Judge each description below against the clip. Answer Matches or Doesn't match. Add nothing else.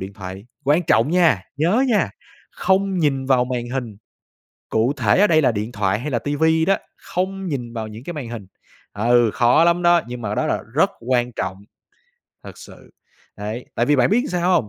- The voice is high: Doesn't match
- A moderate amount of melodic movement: Doesn't match